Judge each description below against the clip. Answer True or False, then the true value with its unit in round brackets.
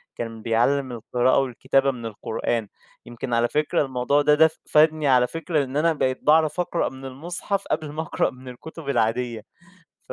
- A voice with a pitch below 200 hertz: True (135 Hz)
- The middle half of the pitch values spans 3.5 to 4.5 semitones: True (4.0 semitones)